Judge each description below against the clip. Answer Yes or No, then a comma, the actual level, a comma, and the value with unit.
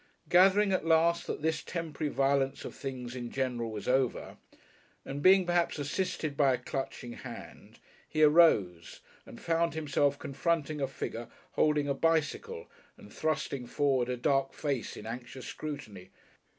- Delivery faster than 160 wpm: No, average, 150 wpm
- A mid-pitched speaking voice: Yes, medium, 145 Hz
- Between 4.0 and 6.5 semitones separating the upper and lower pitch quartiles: Yes, average, 4.3 semitones